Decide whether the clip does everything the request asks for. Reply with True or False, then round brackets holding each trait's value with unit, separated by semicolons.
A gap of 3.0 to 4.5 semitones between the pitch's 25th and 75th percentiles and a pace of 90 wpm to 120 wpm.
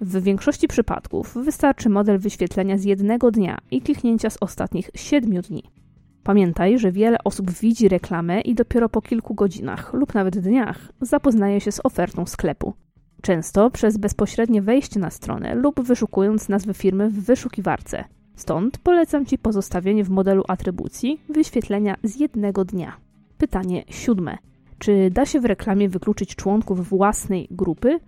False (3.8 semitones; 145 wpm)